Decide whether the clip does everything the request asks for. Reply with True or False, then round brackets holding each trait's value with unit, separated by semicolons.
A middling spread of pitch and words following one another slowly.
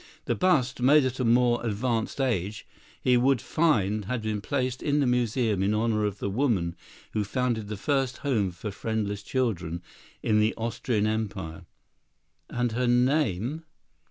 False (3.6 semitones; 155 wpm)